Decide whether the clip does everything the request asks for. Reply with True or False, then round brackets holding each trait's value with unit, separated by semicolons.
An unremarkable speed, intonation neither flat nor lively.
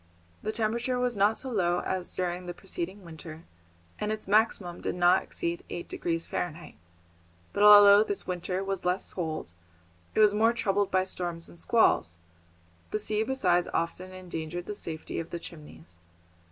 True (165 wpm; 3.4 semitones)